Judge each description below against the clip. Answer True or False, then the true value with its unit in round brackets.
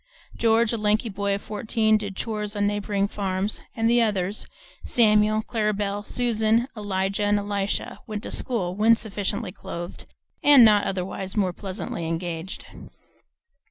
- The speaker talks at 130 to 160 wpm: True (145 wpm)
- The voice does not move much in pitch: True (2.0 semitones)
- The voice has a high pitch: True (205 Hz)